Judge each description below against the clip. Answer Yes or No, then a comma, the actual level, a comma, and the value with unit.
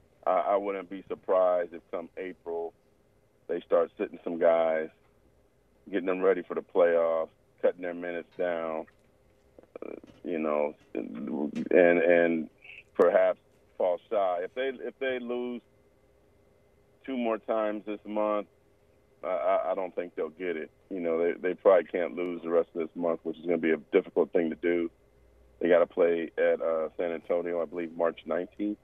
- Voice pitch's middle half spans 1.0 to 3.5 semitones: No, average, 4.1 semitones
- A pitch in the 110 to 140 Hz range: No, very low, 85 Hz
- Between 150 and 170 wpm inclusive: Yes, average, 165 wpm